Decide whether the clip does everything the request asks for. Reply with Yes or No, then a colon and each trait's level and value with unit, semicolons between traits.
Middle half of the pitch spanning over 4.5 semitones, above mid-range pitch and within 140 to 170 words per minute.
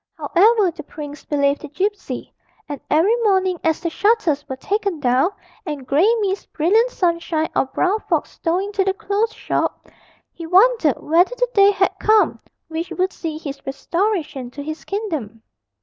Yes: average, 5.2 semitones; very high, 345 Hz; average, 165 wpm